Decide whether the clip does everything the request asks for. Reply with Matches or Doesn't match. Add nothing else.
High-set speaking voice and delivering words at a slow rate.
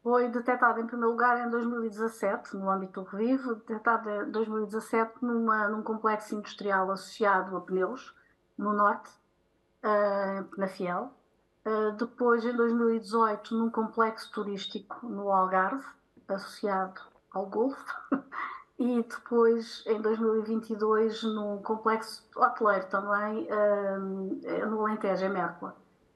Matches